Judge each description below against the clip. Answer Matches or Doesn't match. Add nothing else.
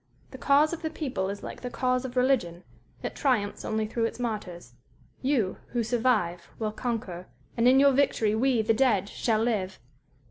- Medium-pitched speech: Doesn't match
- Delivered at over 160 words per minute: Matches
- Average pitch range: Matches